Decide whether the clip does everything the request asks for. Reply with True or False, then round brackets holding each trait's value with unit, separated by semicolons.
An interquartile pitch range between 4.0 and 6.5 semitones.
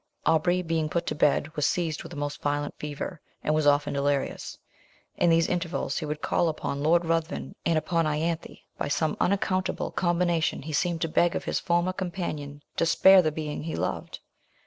False (2.5 semitones)